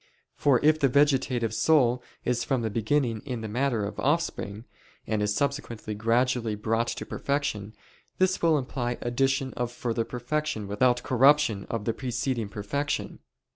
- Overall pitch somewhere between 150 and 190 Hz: No, low, 120 Hz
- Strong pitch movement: No, average, 3.8 semitones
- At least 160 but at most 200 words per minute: No, average, 150 wpm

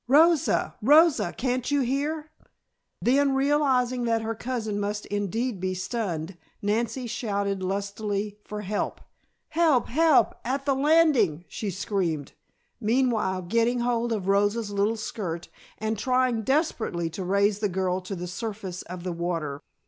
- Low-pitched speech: No, high, 220 Hz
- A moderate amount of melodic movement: Yes, average, 4.8 semitones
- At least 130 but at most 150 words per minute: Yes, average, 140 wpm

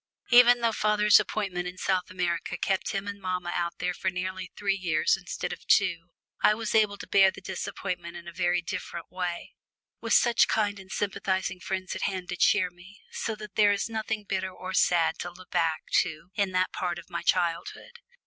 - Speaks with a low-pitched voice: No, medium, 185 Hz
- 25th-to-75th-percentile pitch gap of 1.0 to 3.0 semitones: Yes, narrow, 2.5 semitones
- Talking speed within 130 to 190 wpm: No, average, 200 wpm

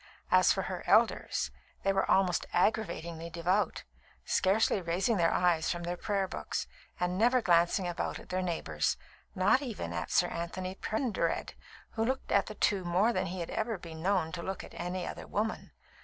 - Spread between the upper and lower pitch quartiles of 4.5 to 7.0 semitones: No, average, 3.0 semitones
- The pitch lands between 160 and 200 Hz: Yes, medium, 185 Hz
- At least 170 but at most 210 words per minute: Yes, average, 180 wpm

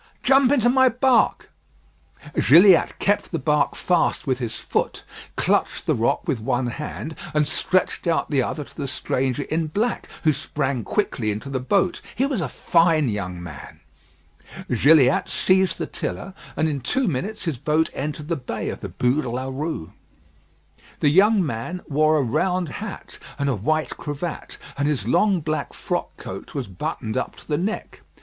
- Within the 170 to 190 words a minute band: Yes, average, 175 wpm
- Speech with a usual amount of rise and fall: No, wide, 5.8 semitones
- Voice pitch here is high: No, medium, 150 Hz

